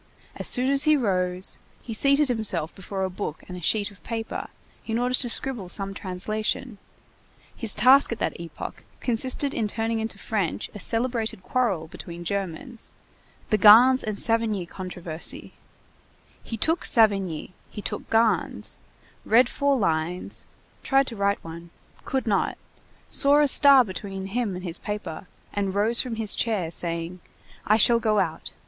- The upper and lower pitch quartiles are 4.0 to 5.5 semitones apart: Yes, average, 4.4 semitones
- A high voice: Yes, high, 215 Hz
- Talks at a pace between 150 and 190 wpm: Yes, average, 155 wpm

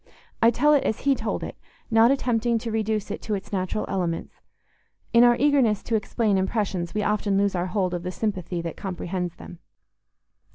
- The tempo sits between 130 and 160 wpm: No, average, 180 wpm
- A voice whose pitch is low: No, high, 210 Hz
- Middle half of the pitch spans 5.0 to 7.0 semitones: No, average, 3.8 semitones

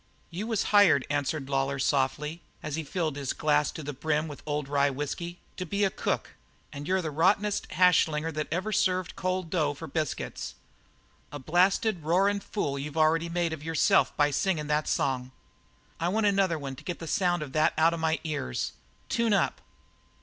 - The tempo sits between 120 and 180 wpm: No, average, 195 wpm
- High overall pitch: No, medium, 160 Hz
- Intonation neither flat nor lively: Yes, average, 3.9 semitones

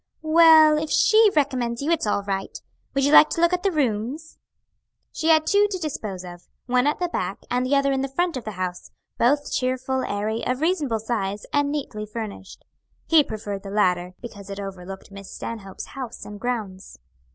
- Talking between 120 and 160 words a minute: No, average, 195 wpm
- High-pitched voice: Yes, very high, 250 Hz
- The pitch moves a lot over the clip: Yes, wide, 6.9 semitones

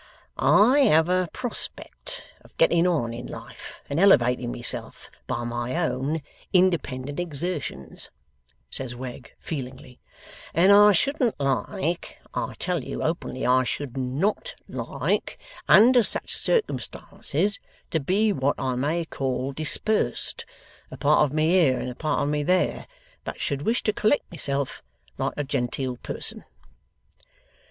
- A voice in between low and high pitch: Yes, medium, 150 Hz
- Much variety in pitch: Yes, wide, 6.1 semitones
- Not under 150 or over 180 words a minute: No, slow, 135 wpm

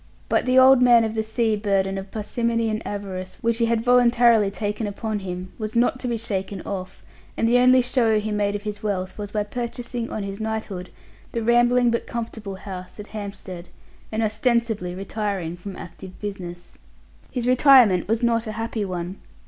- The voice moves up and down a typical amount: Yes, average, 3.0 semitones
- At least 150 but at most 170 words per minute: No, average, 185 wpm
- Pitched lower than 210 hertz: No, high, 215 Hz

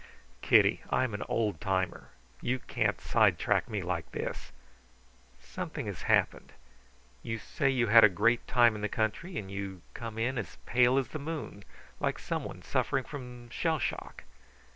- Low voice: Yes, low, 115 Hz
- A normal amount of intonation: Yes, average, 4.2 semitones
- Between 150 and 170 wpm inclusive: Yes, average, 160 wpm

